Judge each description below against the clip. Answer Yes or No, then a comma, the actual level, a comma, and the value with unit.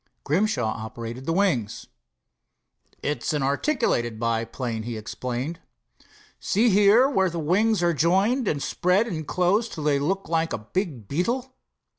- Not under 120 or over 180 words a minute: Yes, average, 140 wpm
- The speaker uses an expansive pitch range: Yes, wide, 8.2 semitones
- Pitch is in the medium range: Yes, medium, 165 Hz